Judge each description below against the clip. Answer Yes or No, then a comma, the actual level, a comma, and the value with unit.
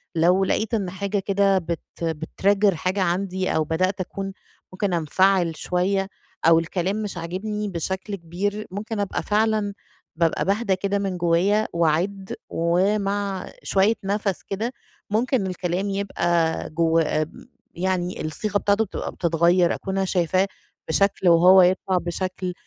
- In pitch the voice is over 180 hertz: Yes, high, 190 Hz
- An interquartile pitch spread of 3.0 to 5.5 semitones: No, narrow, 2.6 semitones